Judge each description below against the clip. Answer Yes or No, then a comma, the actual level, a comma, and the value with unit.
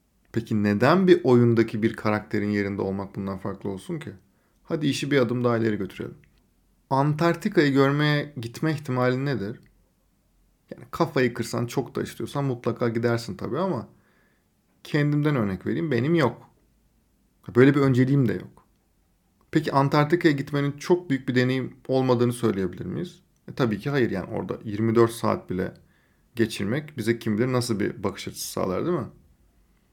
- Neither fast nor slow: No, fast, 150 wpm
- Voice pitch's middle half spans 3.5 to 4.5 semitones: No, average, 4.9 semitones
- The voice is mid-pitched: No, low, 125 Hz